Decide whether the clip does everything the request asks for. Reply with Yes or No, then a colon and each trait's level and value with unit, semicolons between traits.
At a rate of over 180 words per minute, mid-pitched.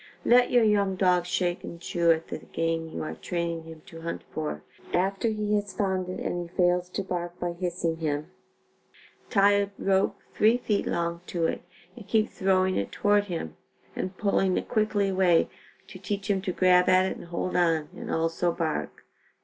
Yes: average, 190 wpm; medium, 180 Hz